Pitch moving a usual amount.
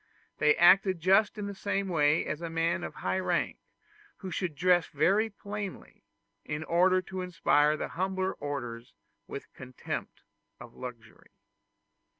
Yes: average, 4.1 semitones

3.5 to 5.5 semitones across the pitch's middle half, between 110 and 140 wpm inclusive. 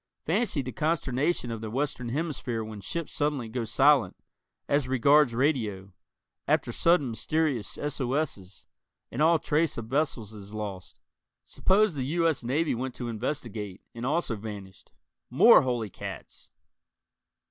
Yes: average, 5.2 semitones; slow, 135 wpm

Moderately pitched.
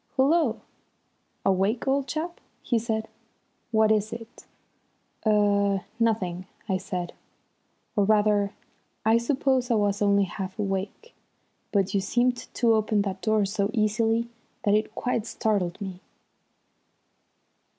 No: high, 215 Hz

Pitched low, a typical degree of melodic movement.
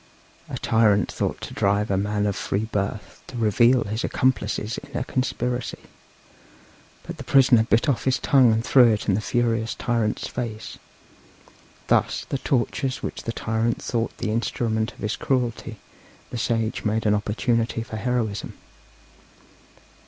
No: low, 115 Hz; narrow, 2.3 semitones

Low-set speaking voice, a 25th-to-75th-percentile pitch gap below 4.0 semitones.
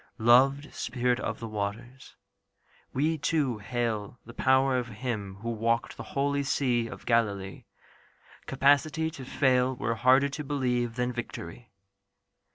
Yes: low, 125 Hz; average, 2.9 semitones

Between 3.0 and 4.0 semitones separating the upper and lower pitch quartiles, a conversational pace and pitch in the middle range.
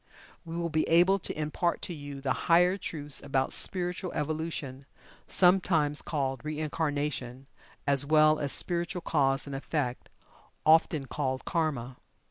No: average, 3.4 semitones; slow, 130 wpm; medium, 150 Hz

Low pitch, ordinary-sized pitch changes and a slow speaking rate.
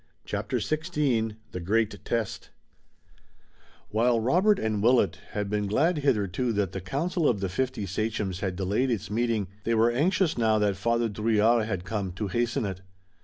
No: low, 110 Hz; average, 3.4 semitones; average, 165 wpm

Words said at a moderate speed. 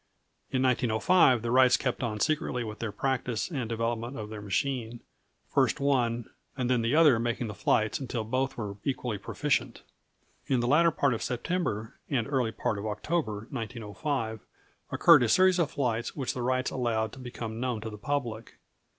Yes: average, 175 wpm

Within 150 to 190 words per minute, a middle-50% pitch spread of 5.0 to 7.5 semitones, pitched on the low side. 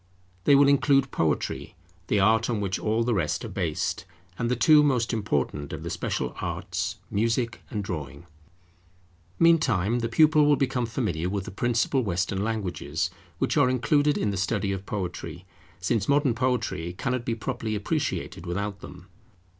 Yes: average, 160 wpm; average, 5.3 semitones; low, 110 Hz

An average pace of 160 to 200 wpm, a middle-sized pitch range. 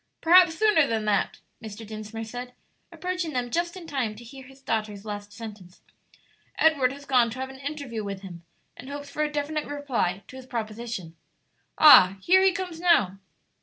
No: average, 180 wpm; wide, 5.9 semitones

